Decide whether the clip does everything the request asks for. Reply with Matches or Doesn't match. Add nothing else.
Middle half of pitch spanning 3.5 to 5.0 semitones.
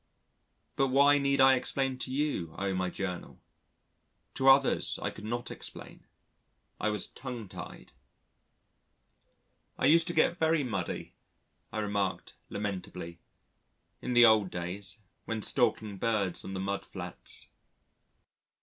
Doesn't match